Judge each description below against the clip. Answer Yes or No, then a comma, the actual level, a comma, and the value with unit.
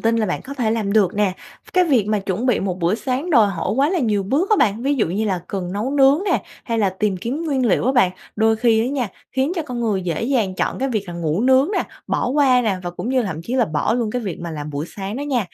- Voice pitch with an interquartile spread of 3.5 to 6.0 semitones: Yes, average, 5.2 semitones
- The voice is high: Yes, high, 225 Hz